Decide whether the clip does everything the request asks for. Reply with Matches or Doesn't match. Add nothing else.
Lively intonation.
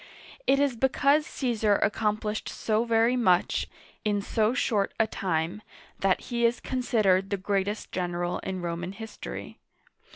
Doesn't match